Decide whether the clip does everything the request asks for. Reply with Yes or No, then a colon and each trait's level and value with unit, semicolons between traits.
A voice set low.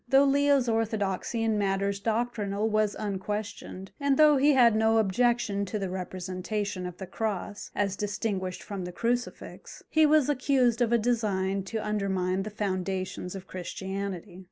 No: high, 210 Hz